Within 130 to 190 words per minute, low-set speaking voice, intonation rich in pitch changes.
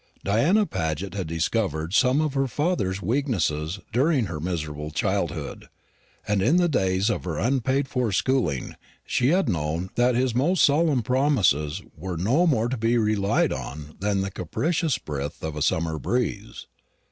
Yes: average, 160 wpm; low, 105 Hz; wide, 8.3 semitones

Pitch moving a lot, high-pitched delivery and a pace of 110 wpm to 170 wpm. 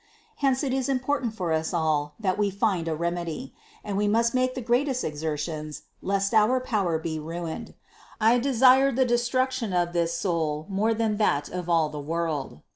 No: wide, 6.9 semitones; high, 195 Hz; average, 180 wpm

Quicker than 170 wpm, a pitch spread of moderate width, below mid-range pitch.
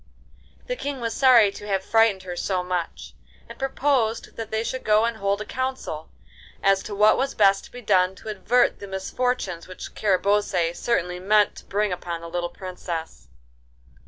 No: average, 180 wpm; average, 3.9 semitones; high, 200 Hz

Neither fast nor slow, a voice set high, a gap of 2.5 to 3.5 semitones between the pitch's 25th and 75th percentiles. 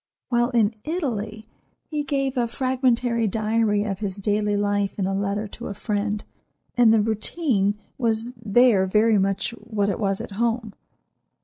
Yes: average, 155 wpm; high, 215 Hz; average, 2.8 semitones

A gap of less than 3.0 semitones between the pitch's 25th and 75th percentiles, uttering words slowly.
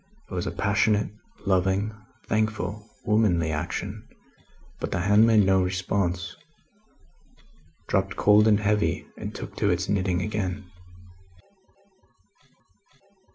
Yes: narrow, 2.5 semitones; slow, 110 wpm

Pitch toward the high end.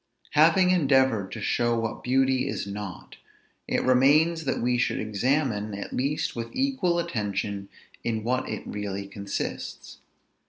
No: low, 125 Hz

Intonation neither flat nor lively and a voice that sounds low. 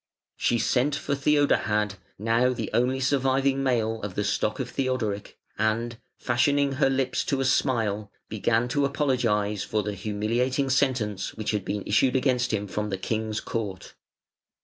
Yes: average, 3.9 semitones; low, 120 Hz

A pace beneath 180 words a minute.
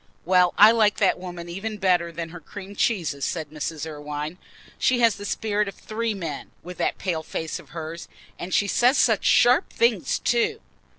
No: average, 185 wpm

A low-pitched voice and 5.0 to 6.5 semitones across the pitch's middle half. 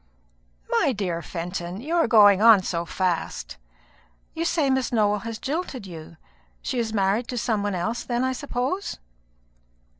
No: high, 220 Hz; wide, 5.4 semitones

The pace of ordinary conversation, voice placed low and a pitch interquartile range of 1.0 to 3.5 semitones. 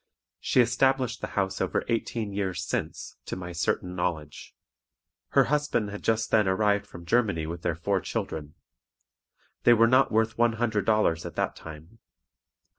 No: average, 160 wpm; low, 105 Hz; average, 4.6 semitones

